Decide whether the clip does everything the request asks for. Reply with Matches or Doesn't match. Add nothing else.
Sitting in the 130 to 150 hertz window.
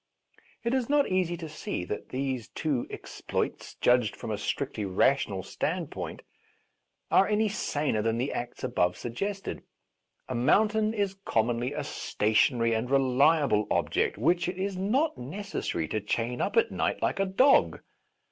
Matches